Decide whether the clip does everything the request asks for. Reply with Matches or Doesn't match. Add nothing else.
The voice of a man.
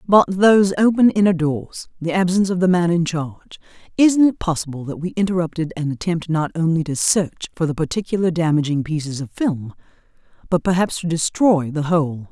Doesn't match